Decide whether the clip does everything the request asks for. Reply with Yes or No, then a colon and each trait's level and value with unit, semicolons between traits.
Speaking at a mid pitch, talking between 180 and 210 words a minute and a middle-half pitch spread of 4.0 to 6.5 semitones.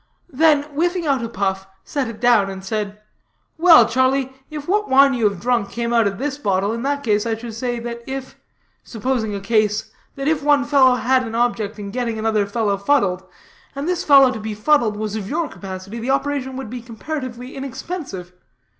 No: high, 240 Hz; average, 200 wpm; average, 4.6 semitones